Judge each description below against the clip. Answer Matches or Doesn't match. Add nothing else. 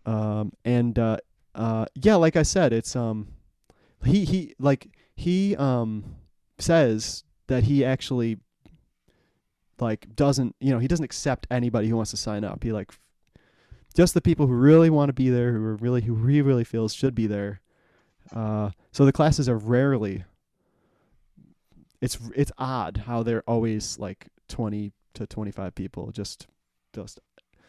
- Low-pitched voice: Matches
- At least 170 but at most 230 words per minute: Doesn't match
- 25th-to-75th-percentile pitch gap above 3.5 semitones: Matches